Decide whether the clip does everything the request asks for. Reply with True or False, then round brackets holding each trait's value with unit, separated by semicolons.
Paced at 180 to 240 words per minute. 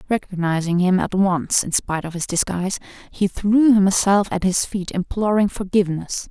False (160 wpm)